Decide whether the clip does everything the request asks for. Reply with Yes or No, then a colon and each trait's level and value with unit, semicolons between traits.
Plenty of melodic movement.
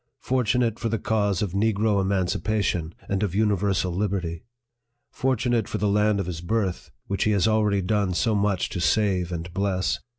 No: average, 2.7 semitones